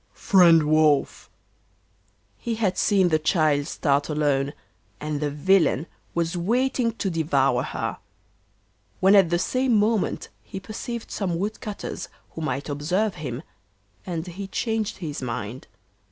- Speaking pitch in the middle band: Yes, medium, 170 Hz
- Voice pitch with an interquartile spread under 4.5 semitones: No, wide, 5.5 semitones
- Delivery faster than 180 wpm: No, slow, 135 wpm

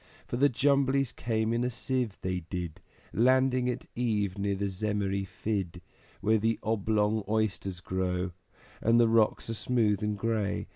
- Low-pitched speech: Yes, low, 110 Hz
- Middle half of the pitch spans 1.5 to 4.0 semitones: Yes, average, 3.2 semitones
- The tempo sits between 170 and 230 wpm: No, average, 155 wpm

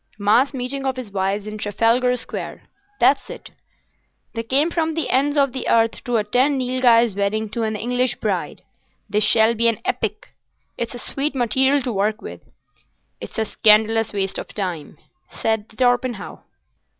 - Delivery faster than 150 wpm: Yes, average, 160 wpm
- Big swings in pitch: No, average, 3.3 semitones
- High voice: Yes, high, 230 Hz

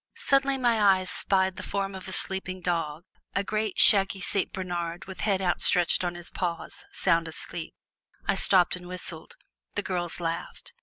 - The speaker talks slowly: No, average, 165 wpm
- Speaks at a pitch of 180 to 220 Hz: Yes, medium, 185 Hz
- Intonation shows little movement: Yes, narrow, 2.0 semitones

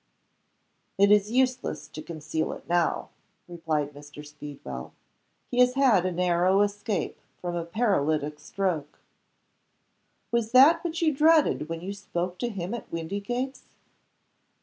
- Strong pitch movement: Yes, wide, 6.9 semitones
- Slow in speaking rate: Yes, slow, 130 wpm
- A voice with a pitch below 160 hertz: No, medium, 185 Hz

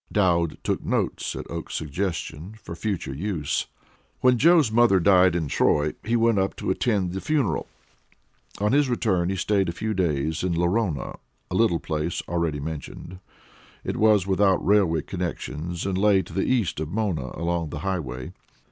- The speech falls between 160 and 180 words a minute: Yes, average, 165 wpm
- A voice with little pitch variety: No, average, 4.1 semitones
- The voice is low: Yes, very low, 90 Hz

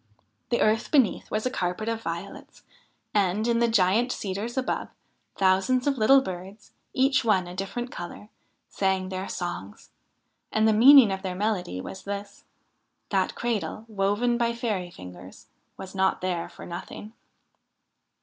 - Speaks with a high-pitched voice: Yes, high, 205 Hz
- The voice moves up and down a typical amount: Yes, average, 3.9 semitones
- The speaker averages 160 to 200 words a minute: No, average, 150 wpm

